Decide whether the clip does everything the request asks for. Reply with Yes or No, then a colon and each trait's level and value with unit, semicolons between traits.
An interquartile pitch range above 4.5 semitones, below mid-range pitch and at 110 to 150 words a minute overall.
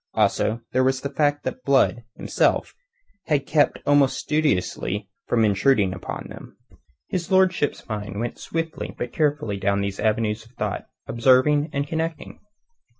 Yes: wide, 5.4 semitones; low, 130 Hz; average, 145 wpm